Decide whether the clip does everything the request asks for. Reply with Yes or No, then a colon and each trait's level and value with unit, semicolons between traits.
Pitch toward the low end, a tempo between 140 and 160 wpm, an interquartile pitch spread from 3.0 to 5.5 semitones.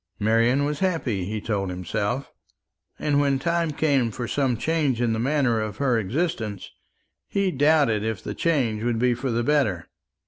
No: low, 125 Hz; average, 170 wpm; average, 4.8 semitones